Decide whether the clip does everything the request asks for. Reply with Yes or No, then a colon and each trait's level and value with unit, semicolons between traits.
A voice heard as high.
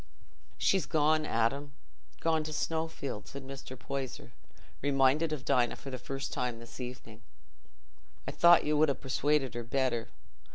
No: low, 135 Hz